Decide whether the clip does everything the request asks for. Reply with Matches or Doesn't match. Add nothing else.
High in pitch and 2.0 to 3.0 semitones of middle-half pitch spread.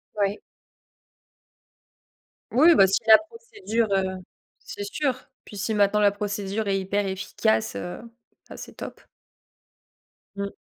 Doesn't match